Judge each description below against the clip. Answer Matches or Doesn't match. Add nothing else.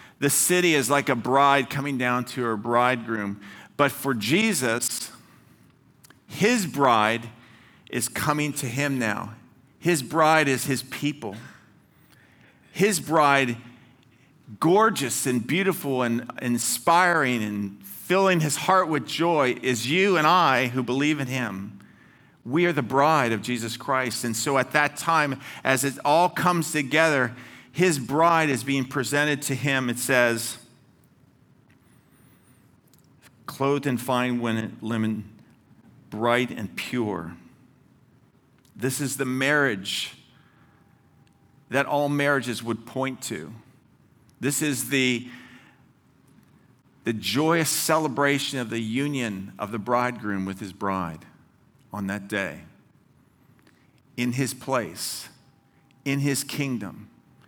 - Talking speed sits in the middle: Doesn't match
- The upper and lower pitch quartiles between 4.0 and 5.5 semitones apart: Doesn't match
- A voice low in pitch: Matches